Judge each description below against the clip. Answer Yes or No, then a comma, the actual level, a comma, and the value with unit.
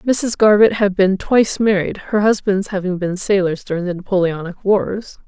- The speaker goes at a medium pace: Yes, average, 170 wpm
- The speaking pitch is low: No, high, 195 Hz